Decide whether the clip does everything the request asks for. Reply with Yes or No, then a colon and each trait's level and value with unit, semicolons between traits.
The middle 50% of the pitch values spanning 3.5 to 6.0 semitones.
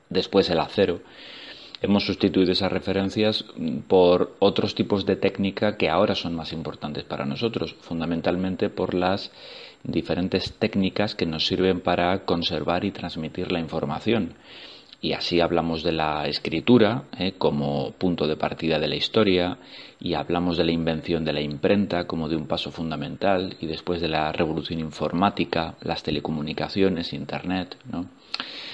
No: average, 3.1 semitones